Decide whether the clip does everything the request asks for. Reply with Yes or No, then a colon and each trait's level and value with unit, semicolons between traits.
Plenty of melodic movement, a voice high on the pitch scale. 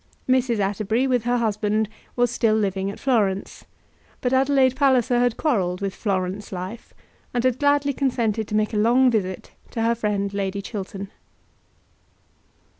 No: average, 3.8 semitones; high, 220 Hz